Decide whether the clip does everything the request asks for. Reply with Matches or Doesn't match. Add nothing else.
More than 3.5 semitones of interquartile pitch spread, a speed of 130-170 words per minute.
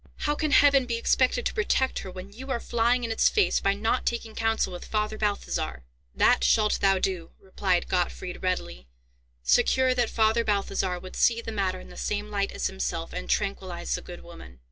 Doesn't match